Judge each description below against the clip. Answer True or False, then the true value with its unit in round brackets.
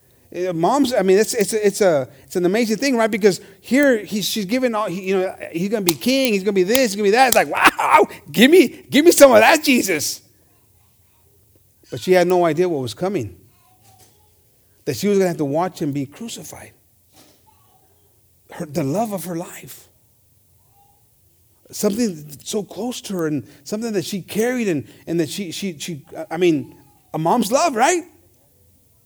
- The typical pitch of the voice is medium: True (170 Hz)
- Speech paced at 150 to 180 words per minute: False (195 wpm)